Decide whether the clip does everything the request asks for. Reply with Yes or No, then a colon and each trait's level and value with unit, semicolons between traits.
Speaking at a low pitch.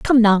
No: high, 225 Hz